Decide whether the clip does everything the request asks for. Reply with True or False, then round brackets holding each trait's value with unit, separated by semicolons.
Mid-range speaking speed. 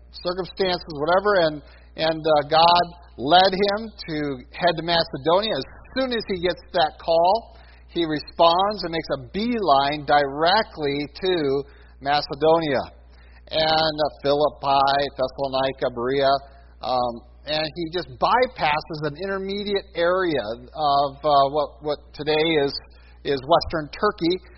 False (120 wpm)